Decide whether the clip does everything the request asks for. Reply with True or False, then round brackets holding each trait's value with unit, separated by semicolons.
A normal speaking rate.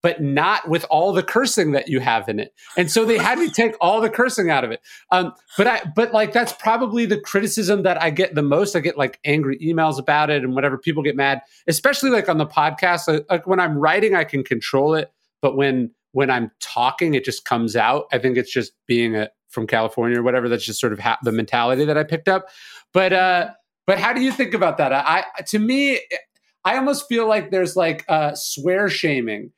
False (235 wpm)